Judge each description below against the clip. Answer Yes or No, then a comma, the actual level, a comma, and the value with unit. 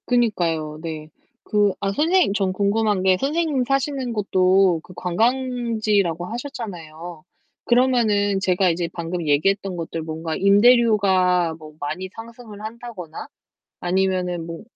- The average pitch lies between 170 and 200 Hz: Yes, high, 195 Hz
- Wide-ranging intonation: No, average, 5.0 semitones